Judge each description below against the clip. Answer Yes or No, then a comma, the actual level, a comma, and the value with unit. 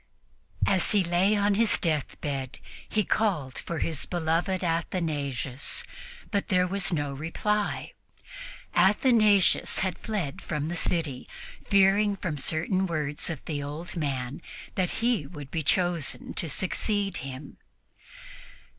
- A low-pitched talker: No, medium, 170 Hz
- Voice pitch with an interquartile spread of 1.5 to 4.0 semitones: No, average, 5.0 semitones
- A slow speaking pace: Yes, slow, 125 wpm